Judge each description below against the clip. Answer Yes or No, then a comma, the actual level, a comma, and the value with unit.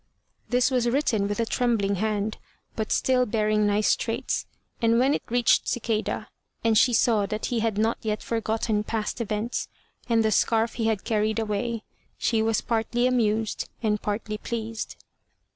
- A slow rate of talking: No, average, 160 wpm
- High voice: Yes, high, 225 Hz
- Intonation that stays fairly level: Yes, narrow, 1.6 semitones